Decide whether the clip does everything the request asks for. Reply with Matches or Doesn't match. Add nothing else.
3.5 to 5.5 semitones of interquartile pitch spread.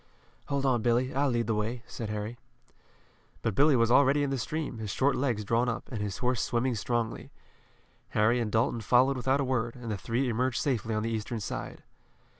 Doesn't match